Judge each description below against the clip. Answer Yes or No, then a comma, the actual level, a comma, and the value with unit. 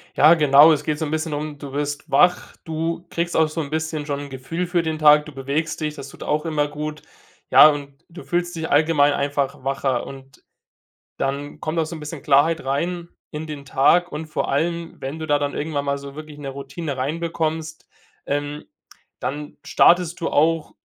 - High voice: No, medium, 150 Hz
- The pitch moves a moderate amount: No, narrow, 2.2 semitones